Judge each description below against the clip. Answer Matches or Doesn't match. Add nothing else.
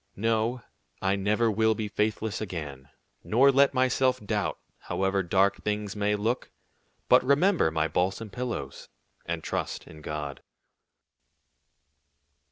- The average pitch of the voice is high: Doesn't match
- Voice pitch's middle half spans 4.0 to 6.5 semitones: Doesn't match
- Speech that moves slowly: Matches